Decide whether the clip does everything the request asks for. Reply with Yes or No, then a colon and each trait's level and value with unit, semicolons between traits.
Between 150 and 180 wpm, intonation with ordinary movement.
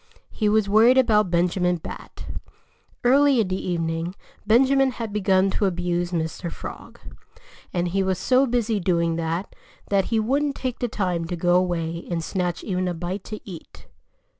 Yes: average, 165 wpm; average, 4.1 semitones